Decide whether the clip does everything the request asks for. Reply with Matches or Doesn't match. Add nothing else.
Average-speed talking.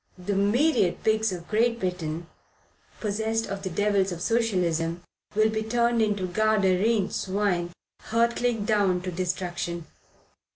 Doesn't match